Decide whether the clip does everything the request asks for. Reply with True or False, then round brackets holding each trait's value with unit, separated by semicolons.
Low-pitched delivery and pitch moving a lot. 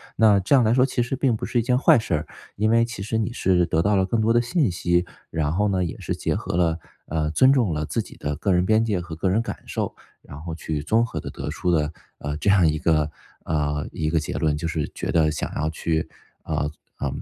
True (90 Hz; 6.0 semitones)